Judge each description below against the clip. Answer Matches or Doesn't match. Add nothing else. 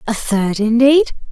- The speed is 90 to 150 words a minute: Matches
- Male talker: Doesn't match